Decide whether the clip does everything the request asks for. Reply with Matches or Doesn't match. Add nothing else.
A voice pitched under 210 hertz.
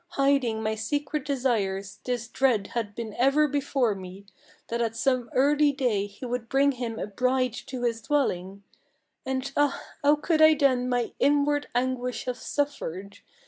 Doesn't match